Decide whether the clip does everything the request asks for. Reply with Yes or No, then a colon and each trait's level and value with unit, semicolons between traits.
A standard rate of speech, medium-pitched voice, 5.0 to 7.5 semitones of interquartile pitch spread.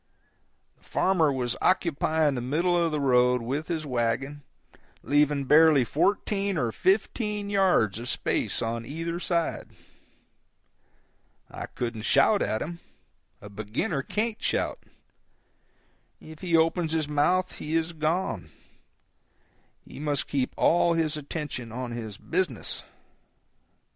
No: slow, 120 wpm; medium, 150 Hz; wide, 5.4 semitones